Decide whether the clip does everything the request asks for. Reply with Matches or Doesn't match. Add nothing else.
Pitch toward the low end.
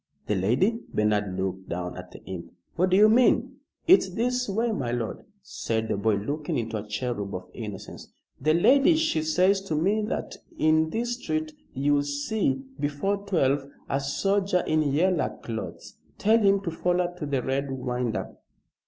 Doesn't match